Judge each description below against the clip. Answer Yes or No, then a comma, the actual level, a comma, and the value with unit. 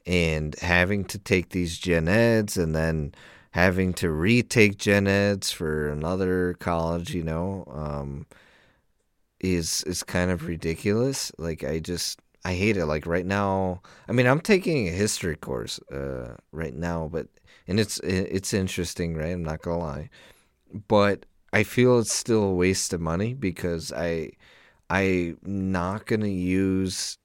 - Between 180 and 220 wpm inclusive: No, average, 150 wpm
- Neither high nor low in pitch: No, very low, 90 Hz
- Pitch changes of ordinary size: Yes, average, 3.2 semitones